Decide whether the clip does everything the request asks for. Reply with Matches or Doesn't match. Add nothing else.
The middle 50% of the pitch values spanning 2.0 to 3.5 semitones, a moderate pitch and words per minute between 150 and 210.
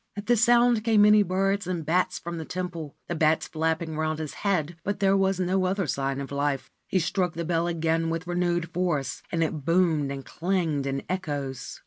Matches